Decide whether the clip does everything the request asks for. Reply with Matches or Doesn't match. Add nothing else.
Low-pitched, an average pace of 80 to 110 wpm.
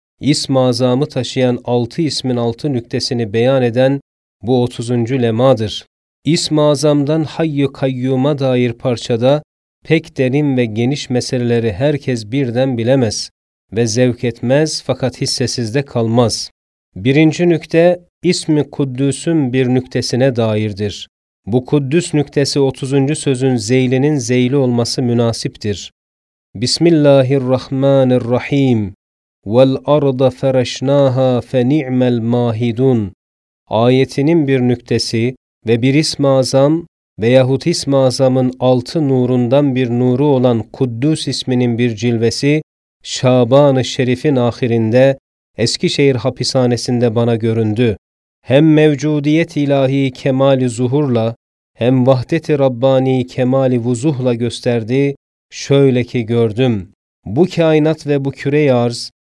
Matches